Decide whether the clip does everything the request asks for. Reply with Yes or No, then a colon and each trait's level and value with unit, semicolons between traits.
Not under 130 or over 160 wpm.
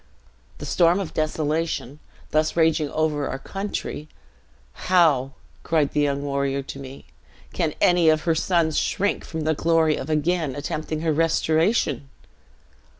Yes: average, 140 wpm